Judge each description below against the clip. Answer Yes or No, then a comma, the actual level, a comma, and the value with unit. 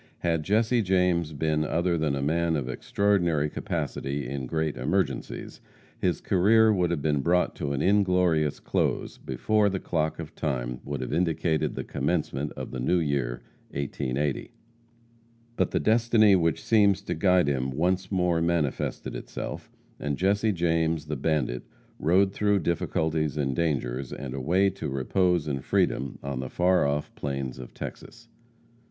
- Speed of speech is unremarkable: Yes, average, 155 wpm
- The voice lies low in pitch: Yes, very low, 80 Hz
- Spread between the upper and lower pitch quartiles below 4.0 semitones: No, average, 4.6 semitones